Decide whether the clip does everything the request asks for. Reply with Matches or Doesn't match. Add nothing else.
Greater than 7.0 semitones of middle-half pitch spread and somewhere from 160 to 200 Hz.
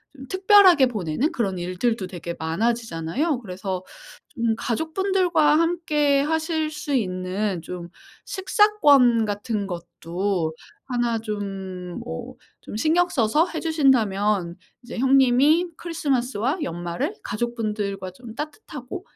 Doesn't match